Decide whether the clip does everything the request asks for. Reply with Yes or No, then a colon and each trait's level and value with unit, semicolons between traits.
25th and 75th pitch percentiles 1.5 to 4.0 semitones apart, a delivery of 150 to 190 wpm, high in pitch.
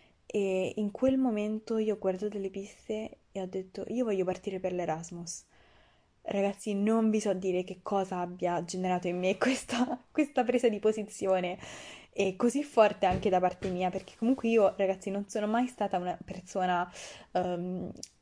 Yes: average, 2.9 semitones; fast, 170 wpm; high, 195 Hz